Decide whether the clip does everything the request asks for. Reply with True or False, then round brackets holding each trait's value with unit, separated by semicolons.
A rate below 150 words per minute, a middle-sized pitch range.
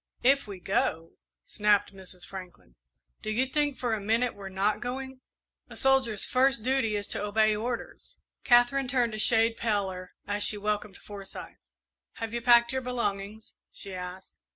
False (160 wpm; 3.8 semitones)